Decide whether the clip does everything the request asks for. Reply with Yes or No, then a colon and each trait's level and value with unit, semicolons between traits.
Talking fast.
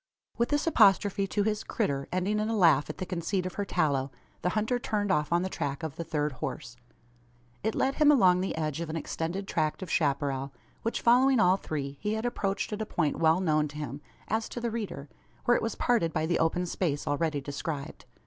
Yes: fast, 220 wpm